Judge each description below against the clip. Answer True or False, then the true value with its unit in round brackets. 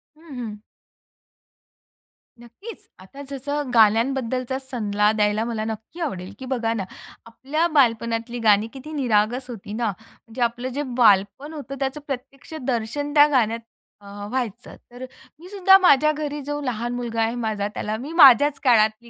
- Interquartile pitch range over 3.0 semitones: True (3.9 semitones)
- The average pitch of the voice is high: True (245 Hz)